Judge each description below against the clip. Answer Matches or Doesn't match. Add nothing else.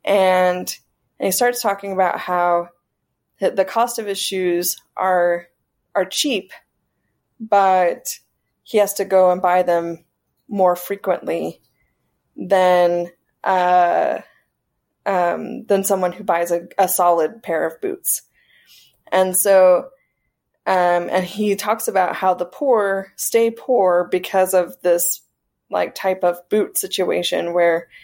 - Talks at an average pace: Doesn't match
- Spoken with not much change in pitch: Matches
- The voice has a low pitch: Doesn't match